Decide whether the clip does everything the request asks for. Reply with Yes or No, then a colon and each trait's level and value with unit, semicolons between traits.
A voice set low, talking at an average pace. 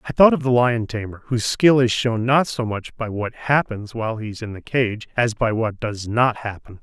No: low, 115 Hz; fast, 245 wpm